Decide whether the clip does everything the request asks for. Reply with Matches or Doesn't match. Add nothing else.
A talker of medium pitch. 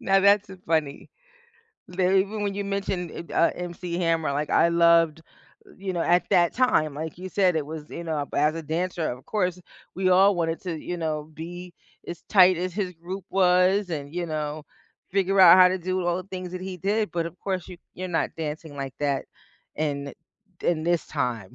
Matches